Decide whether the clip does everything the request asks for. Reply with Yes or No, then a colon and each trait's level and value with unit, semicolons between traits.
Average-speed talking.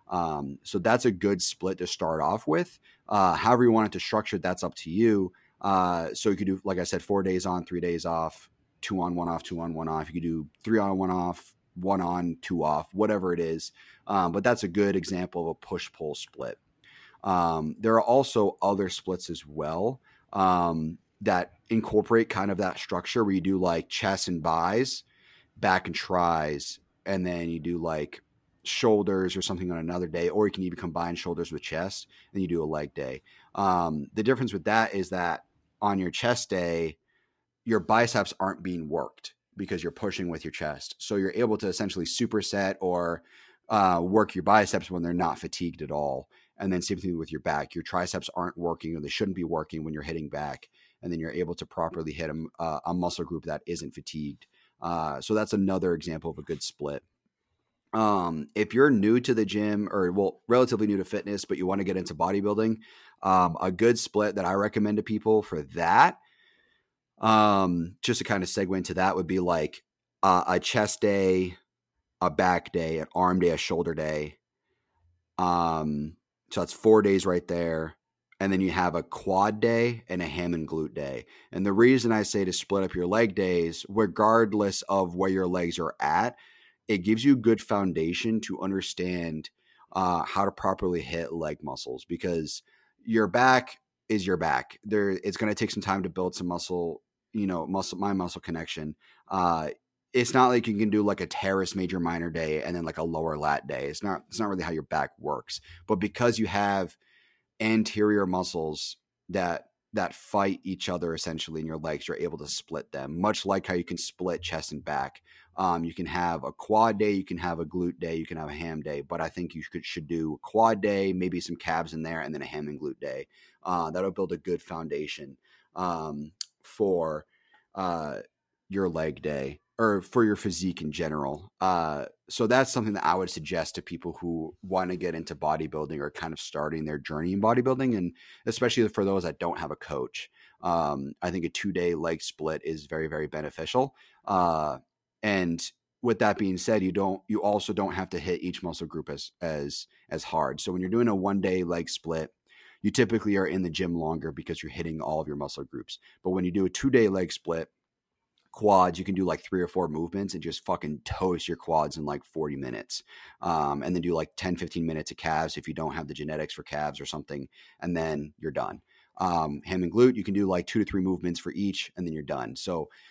No: fast, 210 wpm